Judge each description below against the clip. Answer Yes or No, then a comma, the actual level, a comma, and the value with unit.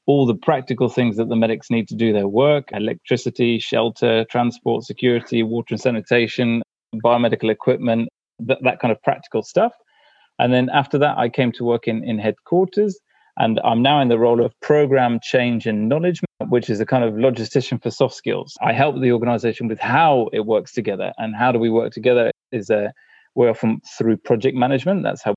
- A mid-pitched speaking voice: No, low, 120 Hz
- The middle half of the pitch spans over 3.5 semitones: No, narrow, 2.6 semitones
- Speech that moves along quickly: No, average, 195 wpm